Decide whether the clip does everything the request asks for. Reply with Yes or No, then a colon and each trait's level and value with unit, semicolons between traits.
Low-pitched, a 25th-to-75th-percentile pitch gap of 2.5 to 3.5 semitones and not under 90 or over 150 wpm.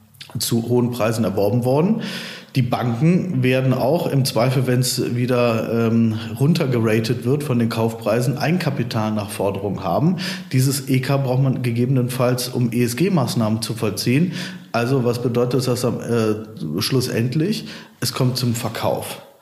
Yes: low, 125 Hz; average, 2.9 semitones; average, 140 wpm